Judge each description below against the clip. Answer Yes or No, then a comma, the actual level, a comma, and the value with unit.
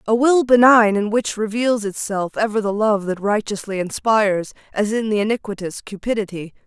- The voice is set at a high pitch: Yes, high, 210 Hz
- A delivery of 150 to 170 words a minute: Yes, average, 160 wpm